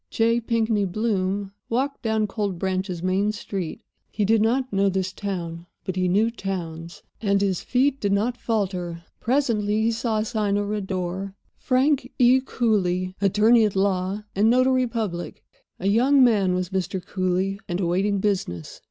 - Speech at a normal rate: Yes, average, 160 wpm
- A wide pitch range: No, average, 3.4 semitones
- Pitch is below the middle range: No, high, 200 Hz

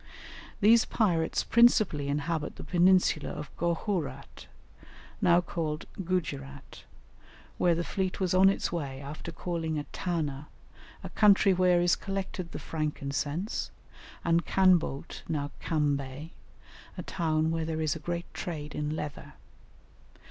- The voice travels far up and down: No, average, 3.4 semitones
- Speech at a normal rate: No, slow, 125 wpm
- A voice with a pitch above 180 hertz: No, medium, 165 Hz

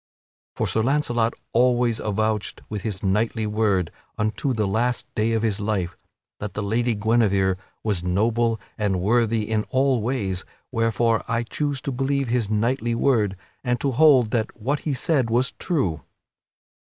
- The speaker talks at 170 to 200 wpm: No, average, 155 wpm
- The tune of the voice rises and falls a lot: No, average, 2.8 semitones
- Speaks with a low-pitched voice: Yes, low, 115 Hz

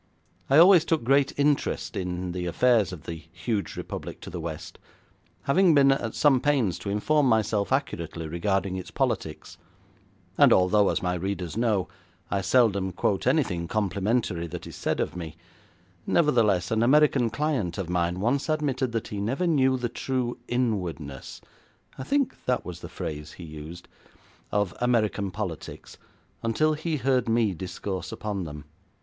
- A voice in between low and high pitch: No, low, 105 Hz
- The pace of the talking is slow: No, average, 155 wpm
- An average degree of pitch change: No, wide, 6.6 semitones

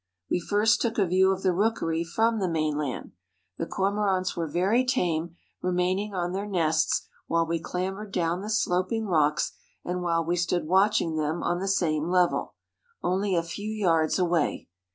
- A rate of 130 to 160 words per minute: No, average, 170 wpm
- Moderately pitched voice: Yes, medium, 180 Hz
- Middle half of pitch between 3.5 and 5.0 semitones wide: No, average, 3.0 semitones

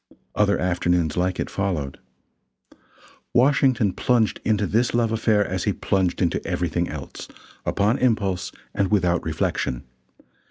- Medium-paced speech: No, slow, 125 wpm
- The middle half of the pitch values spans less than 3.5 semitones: No, average, 3.8 semitones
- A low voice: Yes, very low, 95 Hz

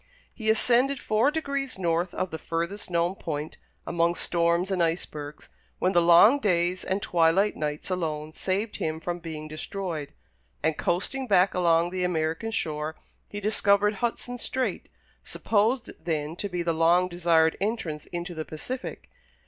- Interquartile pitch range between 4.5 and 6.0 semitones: No, average, 4.0 semitones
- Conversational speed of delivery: Yes, average, 150 wpm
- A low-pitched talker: No, medium, 175 Hz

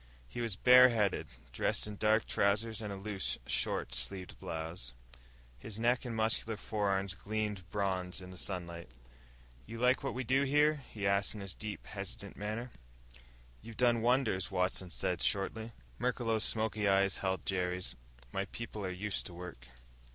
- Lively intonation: No, average, 3.3 semitones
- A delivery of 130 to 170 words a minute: Yes, average, 160 wpm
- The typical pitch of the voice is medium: No, low, 105 Hz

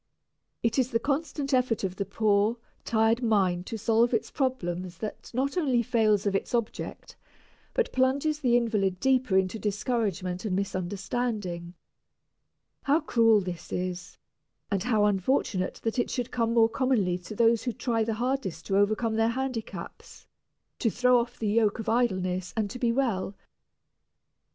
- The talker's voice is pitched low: No, high, 225 Hz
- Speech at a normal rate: Yes, average, 155 wpm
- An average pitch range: Yes, average, 4.1 semitones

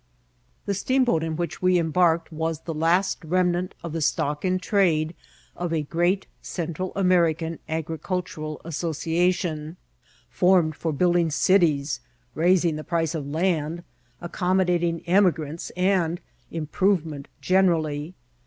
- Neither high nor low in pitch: Yes, medium, 170 Hz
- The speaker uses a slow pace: Yes, slow, 120 wpm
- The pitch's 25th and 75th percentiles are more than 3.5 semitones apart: No, narrow, 2.4 semitones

